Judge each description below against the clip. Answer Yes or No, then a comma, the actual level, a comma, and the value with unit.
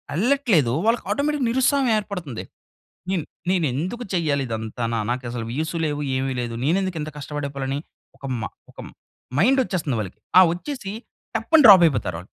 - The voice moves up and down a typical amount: No, wide, 8.9 semitones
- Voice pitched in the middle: Yes, medium, 160 Hz